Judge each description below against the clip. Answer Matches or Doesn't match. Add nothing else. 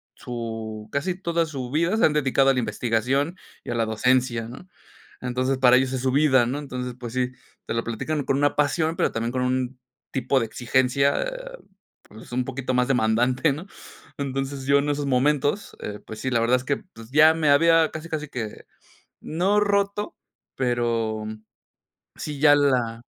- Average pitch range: Matches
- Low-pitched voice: Matches